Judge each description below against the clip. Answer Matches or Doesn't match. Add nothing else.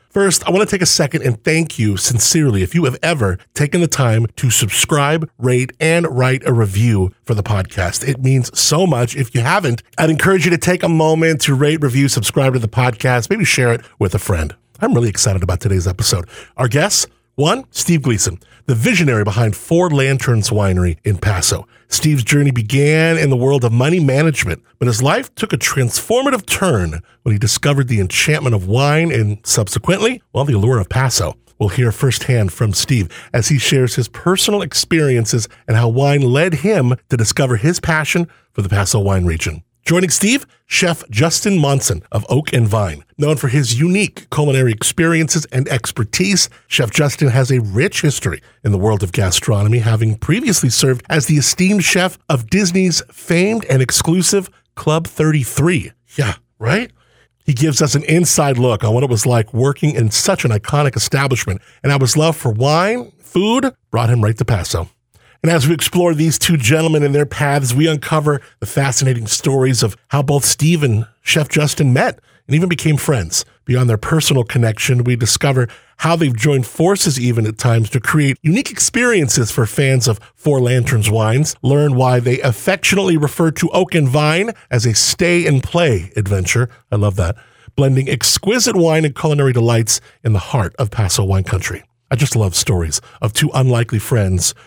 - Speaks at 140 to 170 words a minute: Doesn't match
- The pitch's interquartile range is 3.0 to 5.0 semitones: Doesn't match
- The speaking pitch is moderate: Doesn't match